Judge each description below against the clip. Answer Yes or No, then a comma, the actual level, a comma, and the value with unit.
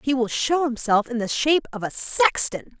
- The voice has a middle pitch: No, very high, 250 Hz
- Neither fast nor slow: No, fast, 215 wpm